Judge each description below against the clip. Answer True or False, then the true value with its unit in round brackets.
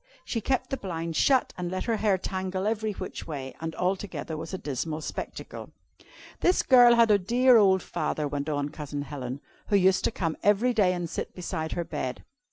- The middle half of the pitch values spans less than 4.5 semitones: False (5.2 semitones)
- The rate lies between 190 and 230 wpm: True (195 wpm)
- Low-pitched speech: False (185 Hz)